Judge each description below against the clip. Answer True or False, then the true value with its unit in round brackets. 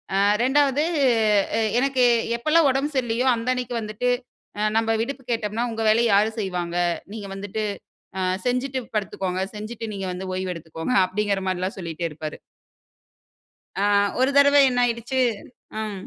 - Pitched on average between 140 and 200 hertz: False (225 Hz)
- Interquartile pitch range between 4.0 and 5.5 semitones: True (4.6 semitones)